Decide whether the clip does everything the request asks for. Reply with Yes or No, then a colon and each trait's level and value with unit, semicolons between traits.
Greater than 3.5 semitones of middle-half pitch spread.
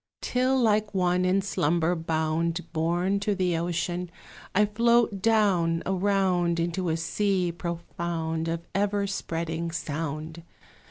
No: average, 3.1 semitones